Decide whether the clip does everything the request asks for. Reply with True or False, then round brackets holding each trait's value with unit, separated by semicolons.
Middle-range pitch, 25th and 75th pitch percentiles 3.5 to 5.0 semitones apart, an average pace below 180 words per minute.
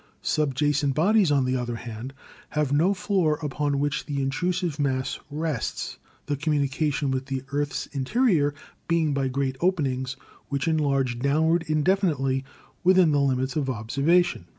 False (145 Hz; 3.1 semitones; 140 wpm)